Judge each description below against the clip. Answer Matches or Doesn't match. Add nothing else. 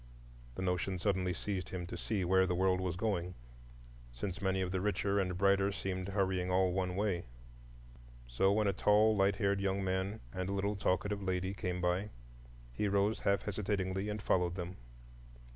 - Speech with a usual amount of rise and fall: Doesn't match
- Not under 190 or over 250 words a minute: Doesn't match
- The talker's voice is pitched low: Matches